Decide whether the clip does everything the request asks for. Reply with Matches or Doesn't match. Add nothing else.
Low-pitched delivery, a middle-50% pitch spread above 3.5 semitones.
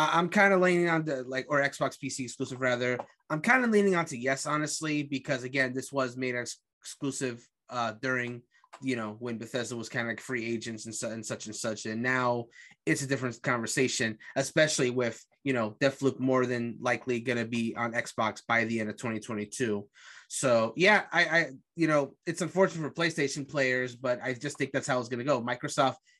Doesn't match